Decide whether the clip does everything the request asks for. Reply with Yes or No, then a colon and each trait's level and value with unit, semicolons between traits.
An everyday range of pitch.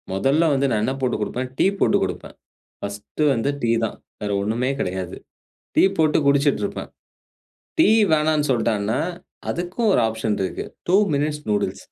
No: wide, 6.0 semitones